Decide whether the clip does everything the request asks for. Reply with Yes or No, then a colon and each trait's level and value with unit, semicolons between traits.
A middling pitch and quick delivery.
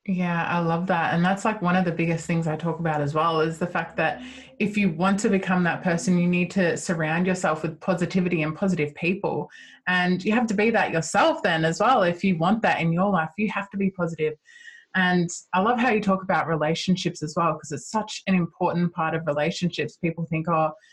Yes: medium, 175 Hz; fast, 230 wpm